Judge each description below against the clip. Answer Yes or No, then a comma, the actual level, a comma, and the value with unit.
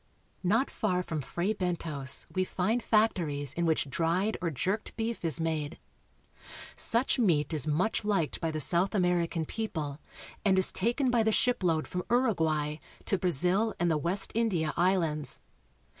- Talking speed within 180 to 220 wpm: No, average, 160 wpm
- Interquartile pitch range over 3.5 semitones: Yes, average, 5.1 semitones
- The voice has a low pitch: No, medium, 180 Hz